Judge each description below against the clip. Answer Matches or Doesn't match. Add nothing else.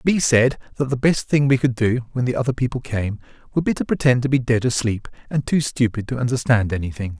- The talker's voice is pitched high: Doesn't match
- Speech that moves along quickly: Matches